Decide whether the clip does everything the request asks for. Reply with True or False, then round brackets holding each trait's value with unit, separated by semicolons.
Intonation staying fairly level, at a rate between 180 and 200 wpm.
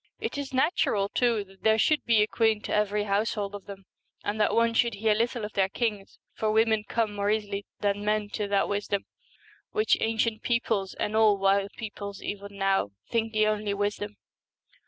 True (1.7 semitones; 190 wpm)